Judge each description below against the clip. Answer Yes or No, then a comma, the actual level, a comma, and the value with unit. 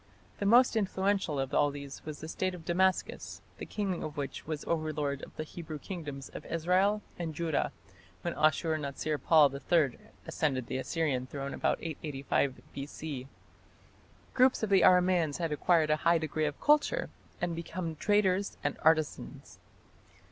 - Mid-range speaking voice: Yes, medium, 160 Hz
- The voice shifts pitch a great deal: No, average, 4.0 semitones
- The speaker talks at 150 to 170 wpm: Yes, average, 155 wpm